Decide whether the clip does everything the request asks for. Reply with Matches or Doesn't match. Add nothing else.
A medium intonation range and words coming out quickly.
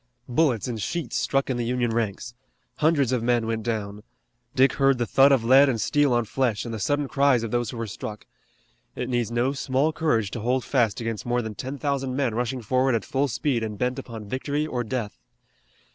Matches